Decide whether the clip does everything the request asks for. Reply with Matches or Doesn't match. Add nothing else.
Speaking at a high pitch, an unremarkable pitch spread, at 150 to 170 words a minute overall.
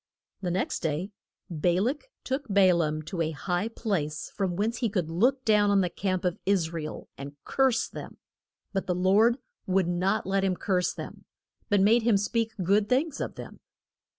Doesn't match